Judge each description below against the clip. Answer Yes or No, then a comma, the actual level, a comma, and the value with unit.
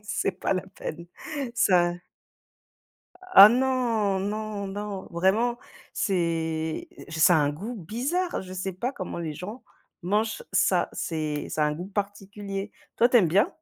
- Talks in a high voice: Yes, high, 195 Hz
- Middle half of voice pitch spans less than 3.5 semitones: No, average, 3.9 semitones